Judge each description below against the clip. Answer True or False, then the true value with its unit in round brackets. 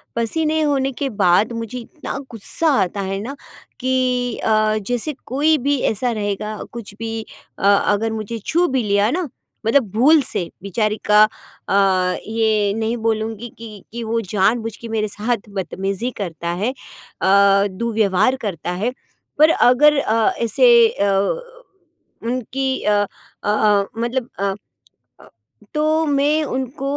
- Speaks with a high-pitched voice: True (225 Hz)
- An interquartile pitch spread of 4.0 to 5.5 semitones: True (4.3 semitones)